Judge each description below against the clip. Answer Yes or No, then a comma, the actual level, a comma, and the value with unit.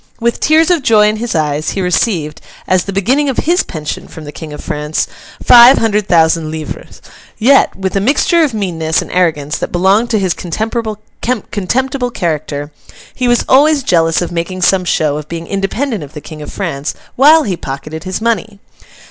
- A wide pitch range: Yes, wide, 6.8 semitones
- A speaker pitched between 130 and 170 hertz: No, high, 190 Hz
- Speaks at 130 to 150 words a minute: No, average, 185 wpm